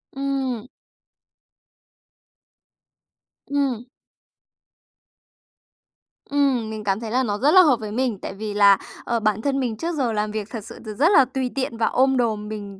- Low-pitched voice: No, high, 235 Hz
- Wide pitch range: No, average, 4.0 semitones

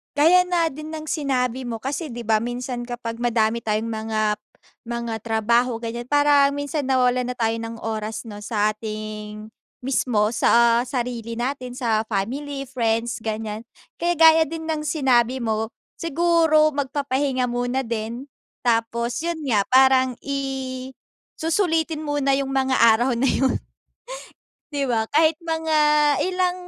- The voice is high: Yes, very high, 250 Hz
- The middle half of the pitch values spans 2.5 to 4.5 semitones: Yes, average, 4.0 semitones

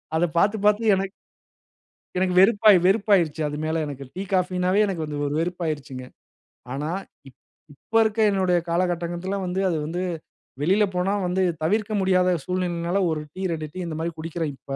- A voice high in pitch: No, medium, 180 Hz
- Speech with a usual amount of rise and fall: Yes, average, 3.0 semitones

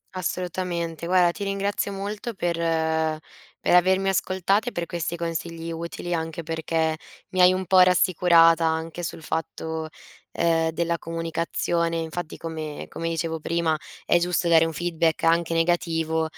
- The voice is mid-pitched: Yes, medium, 165 Hz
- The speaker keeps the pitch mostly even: Yes, narrow, 1.5 semitones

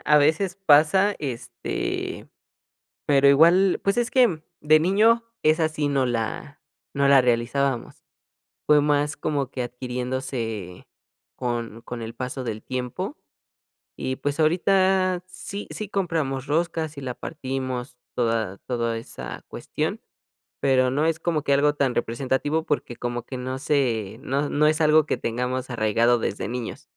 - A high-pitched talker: No, medium, 140 Hz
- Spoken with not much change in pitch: No, average, 4.3 semitones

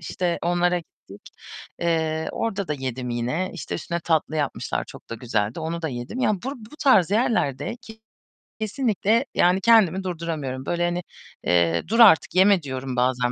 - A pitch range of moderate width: No, wide, 6.6 semitones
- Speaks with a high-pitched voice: No, medium, 170 Hz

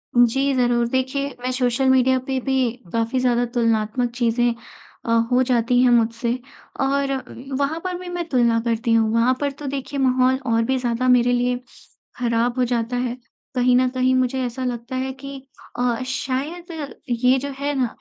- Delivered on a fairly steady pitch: Yes, narrow, 1.8 semitones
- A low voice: No, very high, 250 Hz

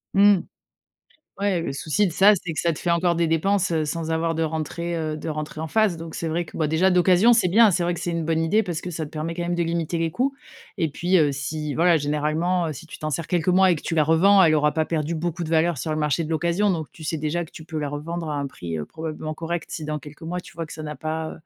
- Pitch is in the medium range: Yes, medium, 165 Hz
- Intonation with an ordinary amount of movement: No, narrow, 2.0 semitones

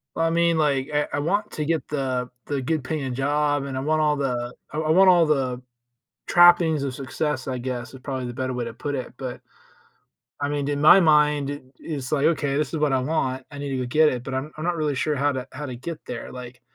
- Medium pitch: Yes, medium, 145 Hz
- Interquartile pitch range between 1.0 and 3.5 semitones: Yes, average, 2.9 semitones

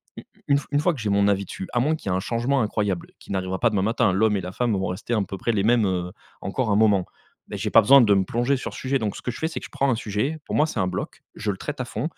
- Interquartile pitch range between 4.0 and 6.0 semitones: Yes, average, 4.6 semitones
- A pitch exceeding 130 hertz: No, low, 110 Hz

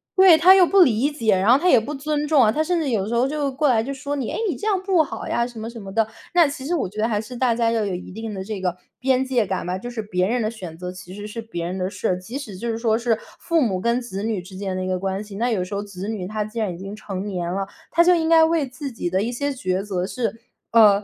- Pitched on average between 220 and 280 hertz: Yes, high, 225 Hz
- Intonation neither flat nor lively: No, wide, 5.8 semitones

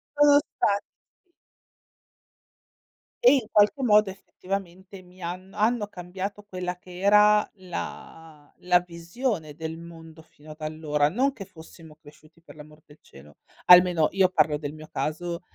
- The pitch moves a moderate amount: Yes, average, 4.2 semitones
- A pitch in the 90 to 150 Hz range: No, medium, 180 Hz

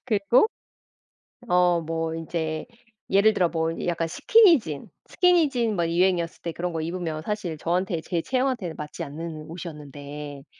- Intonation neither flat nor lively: Yes, average, 3.8 semitones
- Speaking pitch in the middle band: Yes, medium, 170 Hz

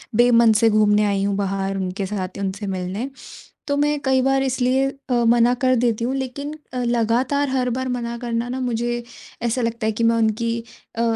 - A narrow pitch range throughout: No, average, 3.0 semitones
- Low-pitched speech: No, high, 235 Hz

